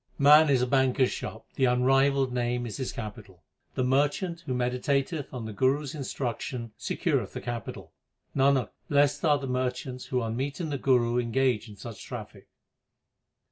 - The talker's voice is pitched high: No, low, 130 Hz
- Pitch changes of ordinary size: No, narrow, 2.3 semitones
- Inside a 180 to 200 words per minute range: No, average, 170 wpm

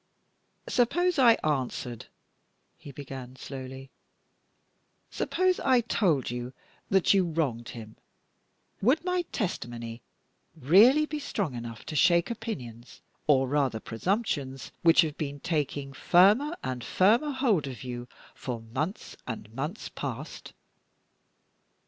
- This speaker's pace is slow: Yes, slow, 115 wpm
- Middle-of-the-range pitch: Yes, medium, 150 Hz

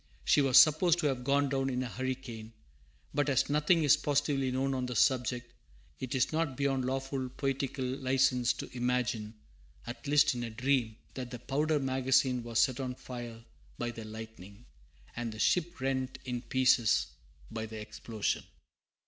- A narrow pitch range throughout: Yes, narrow, 2.3 semitones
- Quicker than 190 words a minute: No, average, 165 wpm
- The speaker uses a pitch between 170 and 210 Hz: No, low, 130 Hz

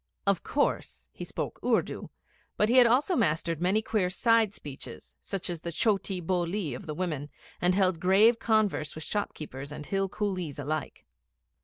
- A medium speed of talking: Yes, average, 160 wpm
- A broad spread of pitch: No, average, 5.0 semitones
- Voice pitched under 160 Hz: No, medium, 185 Hz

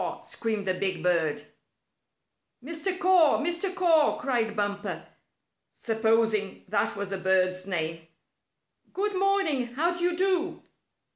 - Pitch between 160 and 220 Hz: No, high, 230 Hz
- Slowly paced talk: Yes, slow, 120 wpm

